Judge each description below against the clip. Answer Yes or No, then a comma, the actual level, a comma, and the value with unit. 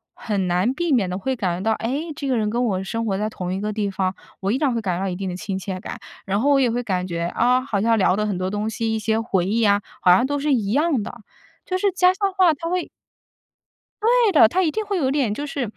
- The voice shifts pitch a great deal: Yes, wide, 6.5 semitones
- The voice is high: Yes, high, 225 Hz